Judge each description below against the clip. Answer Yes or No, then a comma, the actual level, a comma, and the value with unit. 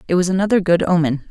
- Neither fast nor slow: No, fast, 230 wpm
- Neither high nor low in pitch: Yes, medium, 175 Hz